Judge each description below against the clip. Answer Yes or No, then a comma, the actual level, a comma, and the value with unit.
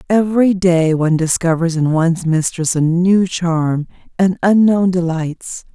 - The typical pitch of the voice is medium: Yes, medium, 175 Hz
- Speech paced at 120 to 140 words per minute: Yes, slow, 135 wpm